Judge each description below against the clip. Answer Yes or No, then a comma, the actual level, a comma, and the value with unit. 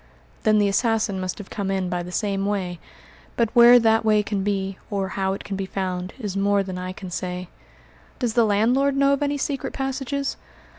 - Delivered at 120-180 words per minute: No, fast, 205 wpm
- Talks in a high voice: Yes, high, 205 Hz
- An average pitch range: Yes, average, 3.7 semitones